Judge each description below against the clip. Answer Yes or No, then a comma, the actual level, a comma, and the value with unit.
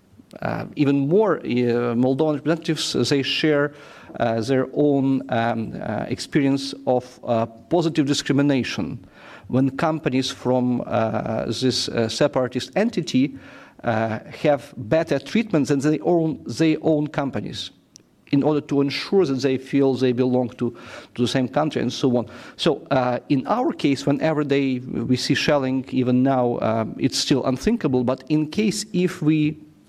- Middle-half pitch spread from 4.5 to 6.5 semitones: No, average, 3.4 semitones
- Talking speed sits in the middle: Yes, average, 150 wpm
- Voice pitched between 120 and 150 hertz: Yes, medium, 140 Hz